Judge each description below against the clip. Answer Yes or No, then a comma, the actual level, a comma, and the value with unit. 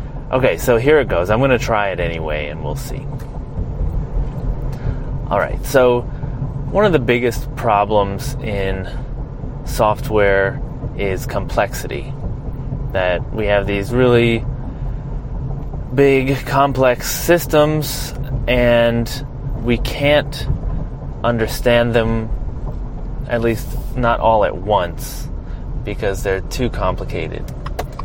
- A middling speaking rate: No, slow, 105 wpm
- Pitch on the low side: Yes, low, 125 Hz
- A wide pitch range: No, average, 3.5 semitones